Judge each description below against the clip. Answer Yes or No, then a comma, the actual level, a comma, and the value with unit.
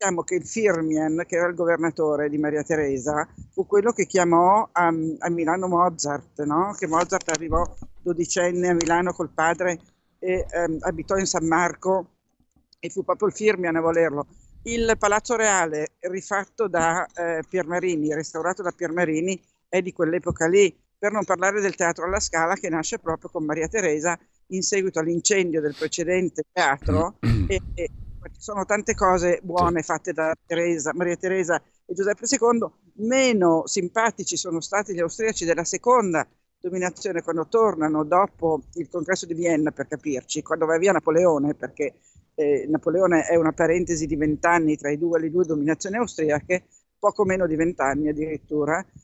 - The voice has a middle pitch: Yes, medium, 170 Hz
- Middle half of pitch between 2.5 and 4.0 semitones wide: Yes, average, 2.8 semitones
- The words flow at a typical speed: Yes, average, 160 wpm